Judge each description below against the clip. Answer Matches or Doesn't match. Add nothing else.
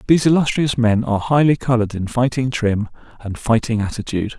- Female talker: Doesn't match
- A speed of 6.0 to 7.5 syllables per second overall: Matches